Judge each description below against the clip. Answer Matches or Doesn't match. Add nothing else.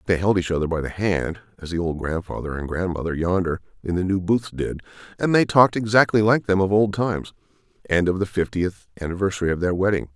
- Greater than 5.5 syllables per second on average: Matches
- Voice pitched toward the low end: Matches